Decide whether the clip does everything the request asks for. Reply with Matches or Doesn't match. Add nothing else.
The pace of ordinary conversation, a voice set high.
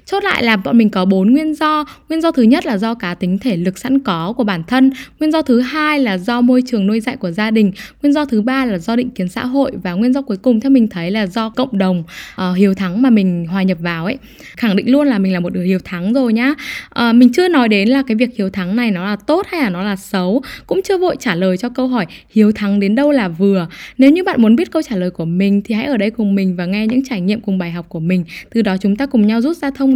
Doesn't match